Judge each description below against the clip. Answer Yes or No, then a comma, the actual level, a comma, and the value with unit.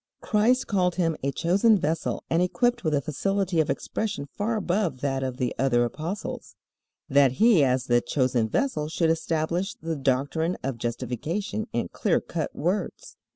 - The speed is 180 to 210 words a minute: No, average, 160 wpm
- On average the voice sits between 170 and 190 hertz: No, medium, 160 Hz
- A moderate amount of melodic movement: No, wide, 6.6 semitones